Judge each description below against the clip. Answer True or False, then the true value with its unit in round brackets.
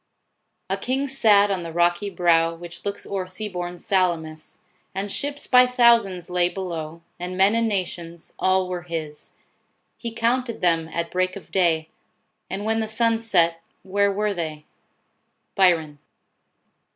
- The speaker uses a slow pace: False (155 wpm)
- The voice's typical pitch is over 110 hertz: True (185 Hz)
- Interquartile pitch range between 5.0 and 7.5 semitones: False (3.7 semitones)